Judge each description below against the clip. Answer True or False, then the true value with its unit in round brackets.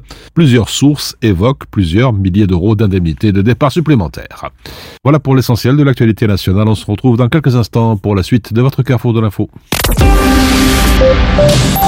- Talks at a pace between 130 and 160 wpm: True (150 wpm)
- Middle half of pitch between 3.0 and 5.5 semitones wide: True (4.1 semitones)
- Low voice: True (115 Hz)